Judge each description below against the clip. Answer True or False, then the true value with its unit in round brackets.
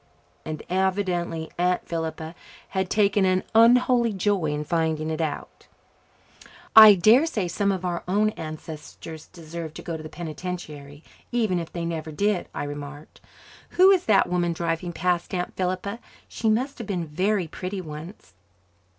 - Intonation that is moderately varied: True (4.1 semitones)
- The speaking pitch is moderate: True (180 Hz)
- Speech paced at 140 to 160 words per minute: True (155 wpm)